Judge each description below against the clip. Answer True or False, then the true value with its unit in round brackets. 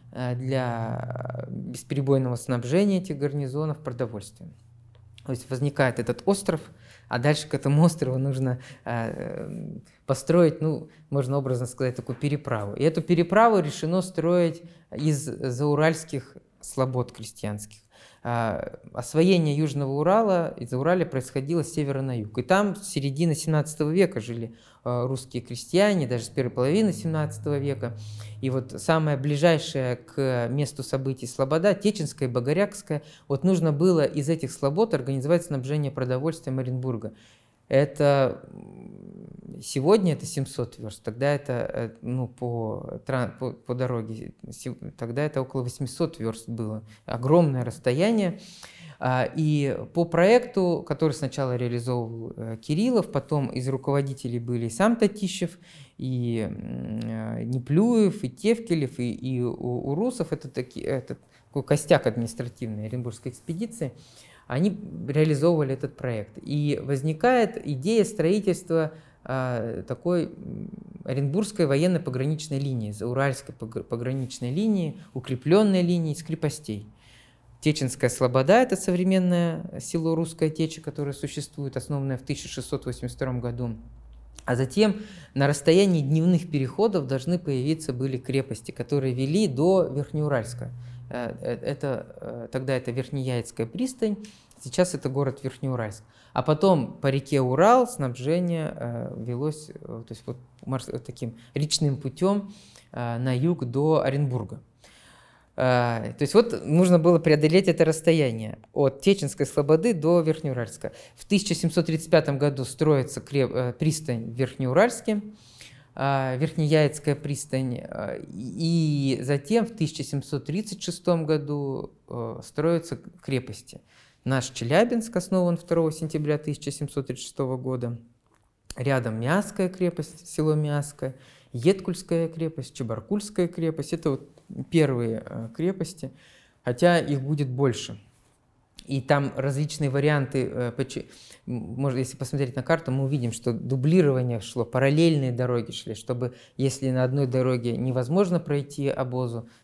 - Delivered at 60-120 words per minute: True (110 wpm)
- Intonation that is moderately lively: True (4.7 semitones)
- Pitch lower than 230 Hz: True (140 Hz)